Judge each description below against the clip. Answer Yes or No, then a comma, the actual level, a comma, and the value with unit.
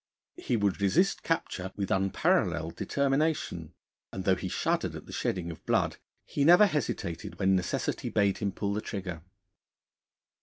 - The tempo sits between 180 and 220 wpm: No, average, 150 wpm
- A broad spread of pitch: Yes, wide, 7.0 semitones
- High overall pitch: No, low, 100 Hz